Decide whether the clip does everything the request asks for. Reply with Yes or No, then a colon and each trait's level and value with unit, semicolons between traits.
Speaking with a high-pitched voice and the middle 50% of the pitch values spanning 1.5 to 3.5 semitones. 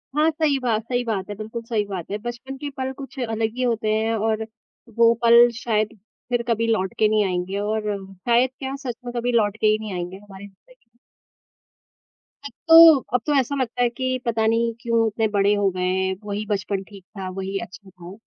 Yes: high, 220 Hz; average, 3.1 semitones